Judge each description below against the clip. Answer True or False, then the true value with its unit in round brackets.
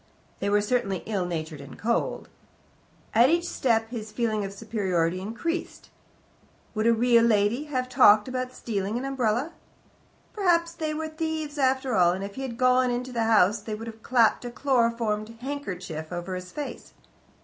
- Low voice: False (230 Hz)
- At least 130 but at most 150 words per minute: False (170 wpm)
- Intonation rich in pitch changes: False (4.0 semitones)